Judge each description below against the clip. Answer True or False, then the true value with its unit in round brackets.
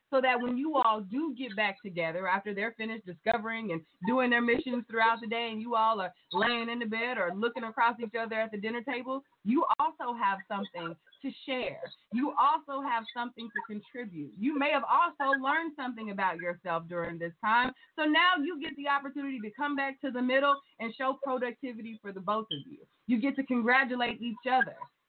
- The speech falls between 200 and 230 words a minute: True (205 wpm)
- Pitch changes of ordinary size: True (3.7 semitones)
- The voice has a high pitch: True (235 Hz)